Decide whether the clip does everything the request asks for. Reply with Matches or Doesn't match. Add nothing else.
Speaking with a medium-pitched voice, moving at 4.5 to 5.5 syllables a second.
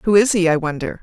Doesn't match